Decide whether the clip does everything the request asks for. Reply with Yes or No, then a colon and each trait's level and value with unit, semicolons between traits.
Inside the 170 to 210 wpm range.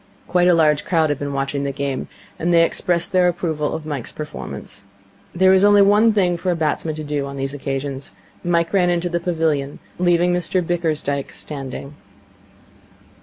Yes: average, 175 wpm